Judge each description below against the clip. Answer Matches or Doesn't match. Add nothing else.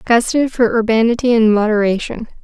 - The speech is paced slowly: Matches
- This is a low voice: Doesn't match